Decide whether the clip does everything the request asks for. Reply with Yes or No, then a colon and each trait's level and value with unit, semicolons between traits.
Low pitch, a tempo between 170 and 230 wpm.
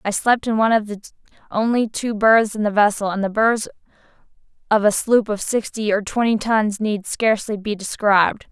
No: high, 215 Hz; average, 185 wpm